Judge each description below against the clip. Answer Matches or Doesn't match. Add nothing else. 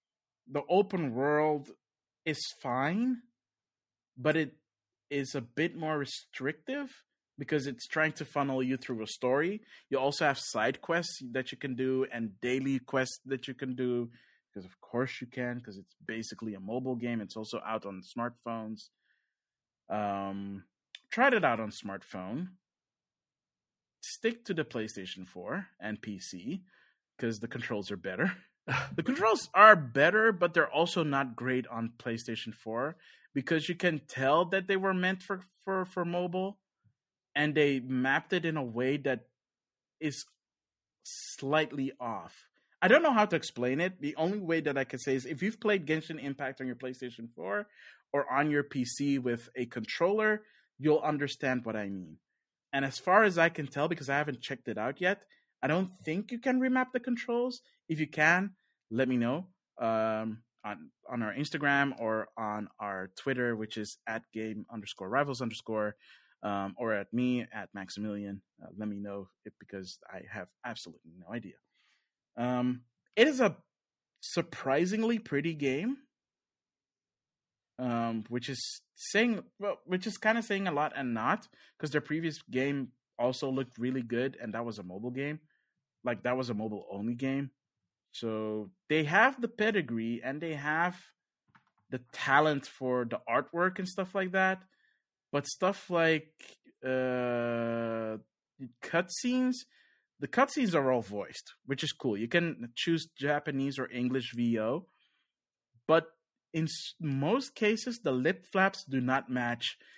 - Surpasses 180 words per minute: Doesn't match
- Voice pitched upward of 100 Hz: Matches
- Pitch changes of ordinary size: Doesn't match